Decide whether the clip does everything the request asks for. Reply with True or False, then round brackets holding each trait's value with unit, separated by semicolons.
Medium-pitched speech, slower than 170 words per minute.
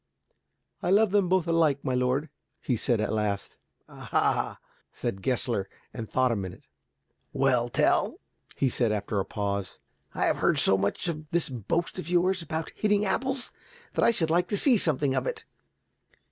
False (150 Hz; 175 wpm)